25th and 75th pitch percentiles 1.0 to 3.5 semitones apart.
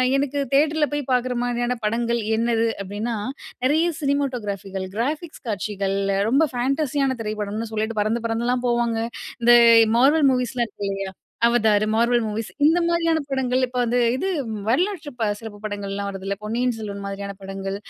No: average, 4.5 semitones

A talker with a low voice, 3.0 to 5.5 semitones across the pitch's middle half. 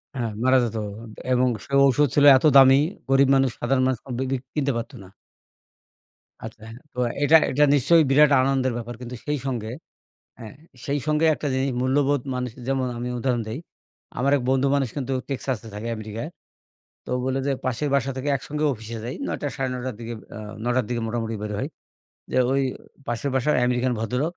No: low, 130 Hz; narrow, 2.5 semitones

